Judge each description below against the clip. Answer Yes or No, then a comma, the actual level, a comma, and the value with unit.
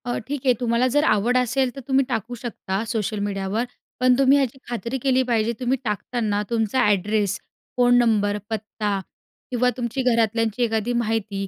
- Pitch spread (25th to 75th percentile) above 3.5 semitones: No, average, 2.9 semitones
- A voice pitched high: Yes, high, 235 Hz